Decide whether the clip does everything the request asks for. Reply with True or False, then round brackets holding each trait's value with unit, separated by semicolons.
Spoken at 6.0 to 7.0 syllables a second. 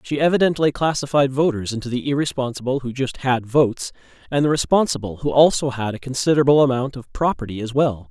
True (6.2 syllables/s)